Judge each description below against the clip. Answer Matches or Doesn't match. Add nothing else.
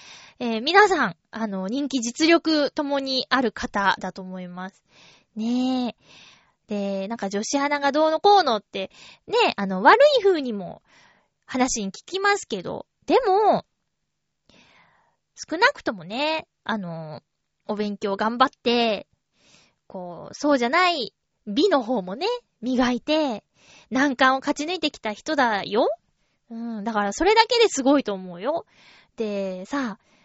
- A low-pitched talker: Doesn't match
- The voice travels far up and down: Matches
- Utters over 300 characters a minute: Doesn't match